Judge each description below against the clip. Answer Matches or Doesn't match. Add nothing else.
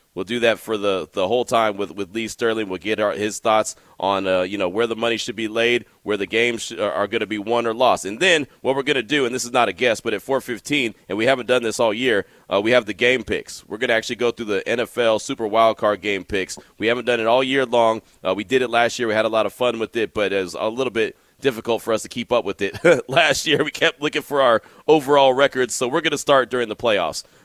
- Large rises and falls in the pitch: Doesn't match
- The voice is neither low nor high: Doesn't match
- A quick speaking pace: Matches